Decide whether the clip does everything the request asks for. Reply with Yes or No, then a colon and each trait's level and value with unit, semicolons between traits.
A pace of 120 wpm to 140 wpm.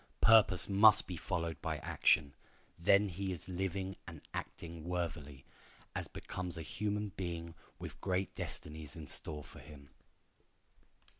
Yes: slow, 135 wpm